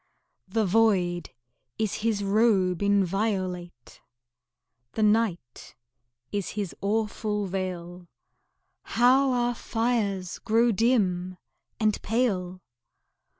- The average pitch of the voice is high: Yes, high, 205 Hz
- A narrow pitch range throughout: No, average, 3.5 semitones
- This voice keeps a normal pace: No, slow, 85 wpm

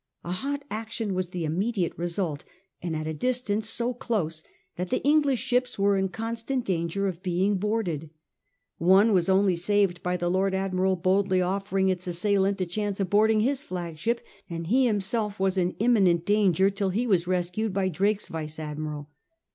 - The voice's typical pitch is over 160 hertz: Yes, high, 190 Hz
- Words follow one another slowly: No, average, 175 wpm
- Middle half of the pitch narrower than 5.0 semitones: Yes, average, 3.4 semitones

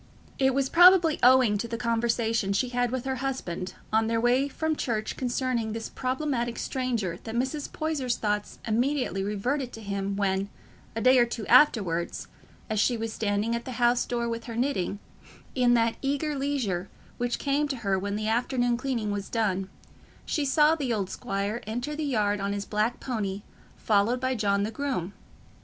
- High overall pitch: Yes, high, 235 Hz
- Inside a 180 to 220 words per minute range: Yes, average, 185 wpm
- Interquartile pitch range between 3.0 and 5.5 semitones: Yes, average, 3.9 semitones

